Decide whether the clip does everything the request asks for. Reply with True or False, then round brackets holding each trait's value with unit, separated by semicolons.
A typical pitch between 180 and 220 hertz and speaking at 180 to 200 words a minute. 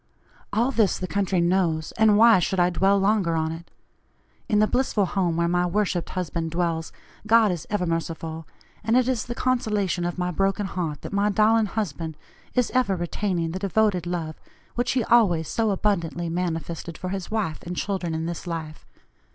True (185 Hz; 185 wpm)